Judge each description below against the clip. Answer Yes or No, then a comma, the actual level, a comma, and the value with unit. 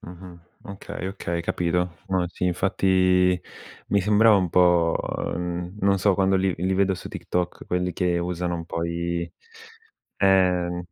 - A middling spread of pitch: No, narrow, 1.5 semitones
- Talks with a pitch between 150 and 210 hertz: No, very low, 90 Hz